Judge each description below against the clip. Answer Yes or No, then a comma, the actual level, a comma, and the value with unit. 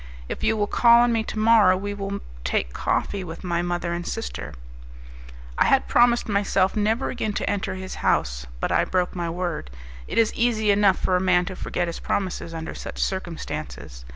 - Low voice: No, high, 190 Hz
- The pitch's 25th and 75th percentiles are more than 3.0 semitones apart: Yes, average, 3.6 semitones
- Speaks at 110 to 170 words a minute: No, average, 195 wpm